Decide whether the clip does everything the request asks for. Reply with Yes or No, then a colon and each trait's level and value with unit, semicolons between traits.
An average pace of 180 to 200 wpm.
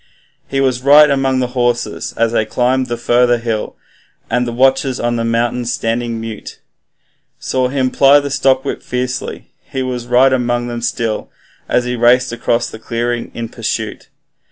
No: average, 165 wpm